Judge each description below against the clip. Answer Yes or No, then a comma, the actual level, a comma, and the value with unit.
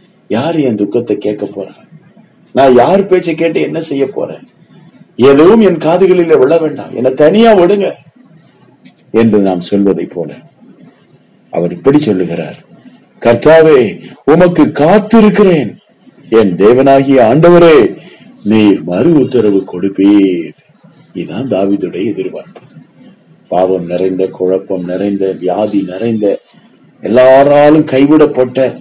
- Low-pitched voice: Yes, low, 130 Hz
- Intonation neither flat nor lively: No, wide, 8.7 semitones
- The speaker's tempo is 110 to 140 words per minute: No, average, 95 wpm